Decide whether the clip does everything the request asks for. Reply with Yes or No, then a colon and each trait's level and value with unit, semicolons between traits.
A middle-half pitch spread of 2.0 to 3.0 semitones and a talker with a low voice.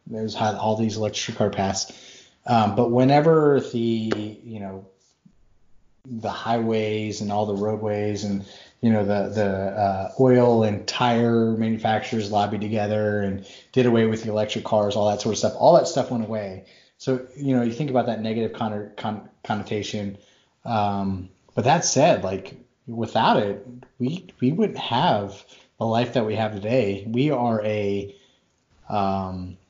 Yes: narrow, 2.5 semitones; low, 110 Hz